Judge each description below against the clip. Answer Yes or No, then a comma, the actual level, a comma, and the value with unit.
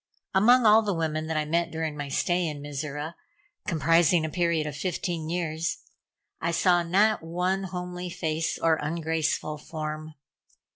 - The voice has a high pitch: No, medium, 165 Hz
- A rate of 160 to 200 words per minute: No, average, 150 wpm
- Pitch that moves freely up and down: No, narrow, 2.4 semitones